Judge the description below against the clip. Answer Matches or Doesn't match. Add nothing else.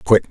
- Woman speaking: Doesn't match